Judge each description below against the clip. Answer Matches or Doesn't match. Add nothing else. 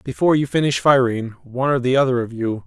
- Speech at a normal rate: Doesn't match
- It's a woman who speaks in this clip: Doesn't match